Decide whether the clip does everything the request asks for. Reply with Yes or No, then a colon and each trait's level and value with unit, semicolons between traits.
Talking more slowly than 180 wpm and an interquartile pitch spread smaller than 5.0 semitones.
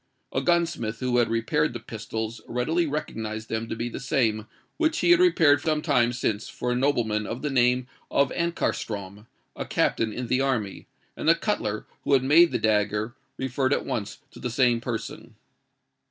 No: average, 185 wpm; average, 4.5 semitones